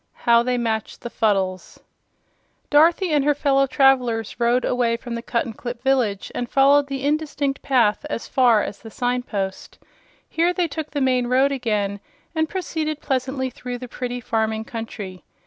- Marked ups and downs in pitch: No, average, 3.4 semitones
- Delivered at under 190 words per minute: Yes, average, 165 wpm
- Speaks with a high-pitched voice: Yes, very high, 250 Hz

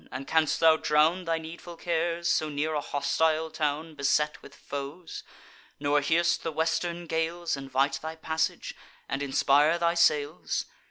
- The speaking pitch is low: No, medium, 160 Hz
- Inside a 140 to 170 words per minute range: Yes, average, 150 wpm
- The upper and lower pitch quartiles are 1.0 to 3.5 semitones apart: Yes, narrow, 2.4 semitones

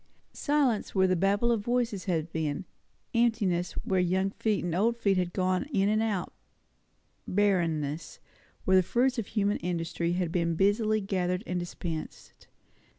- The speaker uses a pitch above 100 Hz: Yes, high, 190 Hz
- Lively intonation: No, average, 3.6 semitones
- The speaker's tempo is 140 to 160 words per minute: Yes, average, 155 wpm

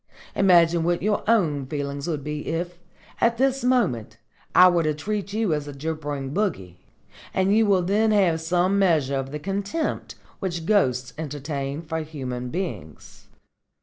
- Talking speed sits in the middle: Yes, average, 155 wpm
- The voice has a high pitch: No, medium, 165 Hz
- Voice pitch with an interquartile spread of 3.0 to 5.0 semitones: No, wide, 5.5 semitones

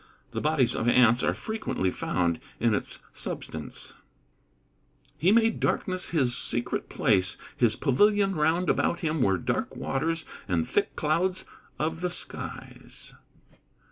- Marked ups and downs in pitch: Yes, wide, 7.3 semitones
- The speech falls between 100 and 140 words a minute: Yes, slow, 135 wpm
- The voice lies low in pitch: No, medium, 150 Hz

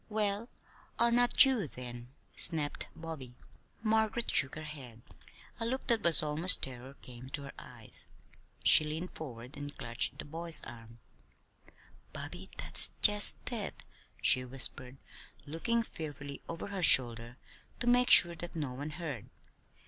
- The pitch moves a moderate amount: No, wide, 7.7 semitones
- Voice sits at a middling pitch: Yes, medium, 155 Hz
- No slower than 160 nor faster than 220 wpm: No, average, 140 wpm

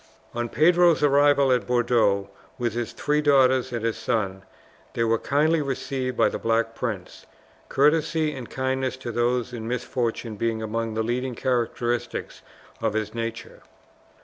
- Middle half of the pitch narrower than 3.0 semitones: Yes, narrow, 2.6 semitones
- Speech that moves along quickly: No, average, 150 wpm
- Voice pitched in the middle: No, low, 120 Hz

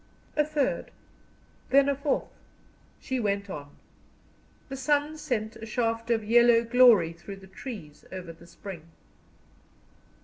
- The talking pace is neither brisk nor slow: No, slow, 130 wpm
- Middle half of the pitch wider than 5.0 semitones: Yes, wide, 5.5 semitones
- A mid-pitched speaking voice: No, high, 230 Hz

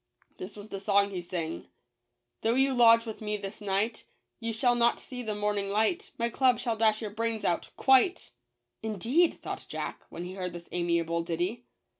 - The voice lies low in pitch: No, high, 210 Hz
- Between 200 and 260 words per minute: Yes, fast, 205 wpm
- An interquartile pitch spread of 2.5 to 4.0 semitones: No, average, 4.7 semitones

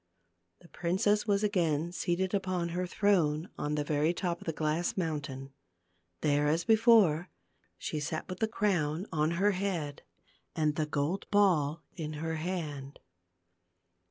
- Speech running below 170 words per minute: Yes, average, 145 wpm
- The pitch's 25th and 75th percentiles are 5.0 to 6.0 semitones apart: No, average, 3.8 semitones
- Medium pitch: Yes, medium, 170 Hz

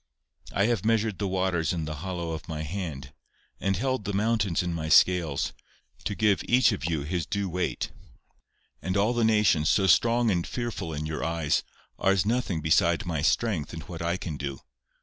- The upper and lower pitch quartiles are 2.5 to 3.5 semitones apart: No, average, 4.4 semitones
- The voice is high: No, very low, 90 Hz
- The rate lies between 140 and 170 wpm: No, average, 185 wpm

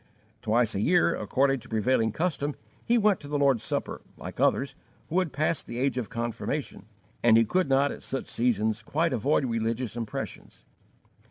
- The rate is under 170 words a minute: No, average, 175 wpm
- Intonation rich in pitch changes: No, average, 4.5 semitones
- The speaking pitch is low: Yes, low, 130 Hz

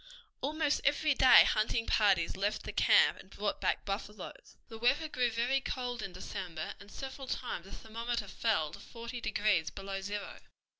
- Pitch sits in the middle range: No, high, 225 Hz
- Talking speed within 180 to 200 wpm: No, average, 165 wpm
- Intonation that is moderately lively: Yes, average, 4.3 semitones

